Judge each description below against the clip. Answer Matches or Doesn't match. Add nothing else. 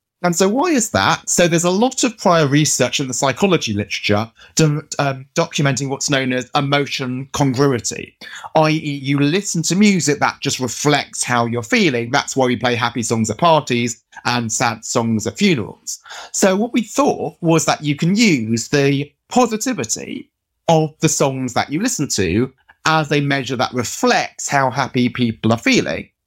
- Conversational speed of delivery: Matches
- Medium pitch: Matches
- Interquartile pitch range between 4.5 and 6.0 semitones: Matches